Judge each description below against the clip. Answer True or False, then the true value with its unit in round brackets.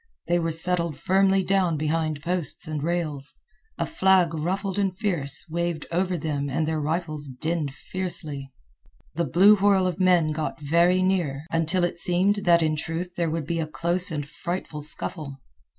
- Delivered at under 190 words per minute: True (165 wpm)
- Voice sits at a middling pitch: True (170 Hz)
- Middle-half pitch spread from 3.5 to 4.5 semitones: False (2.9 semitones)